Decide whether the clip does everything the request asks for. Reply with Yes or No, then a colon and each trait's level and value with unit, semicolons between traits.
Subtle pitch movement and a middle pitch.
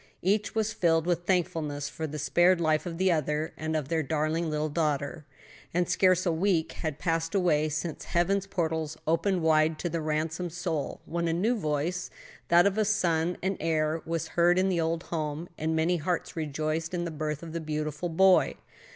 Yes: narrow, 2.3 semitones; medium, 165 Hz